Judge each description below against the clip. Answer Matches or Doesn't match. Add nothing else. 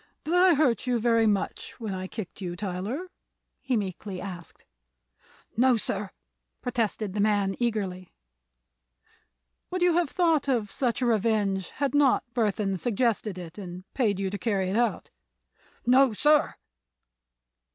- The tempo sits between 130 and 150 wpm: Matches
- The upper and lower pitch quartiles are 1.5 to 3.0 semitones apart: Doesn't match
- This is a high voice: Matches